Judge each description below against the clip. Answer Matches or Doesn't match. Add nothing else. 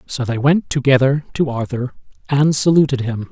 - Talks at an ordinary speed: Matches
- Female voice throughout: Doesn't match